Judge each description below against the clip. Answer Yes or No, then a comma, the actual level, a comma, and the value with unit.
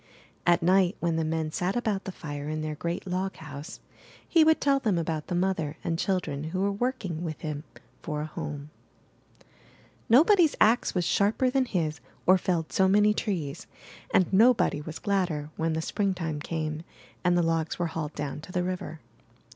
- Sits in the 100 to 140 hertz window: No, medium, 175 Hz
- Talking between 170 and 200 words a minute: Yes, average, 180 wpm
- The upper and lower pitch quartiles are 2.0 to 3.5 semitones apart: No, average, 4.0 semitones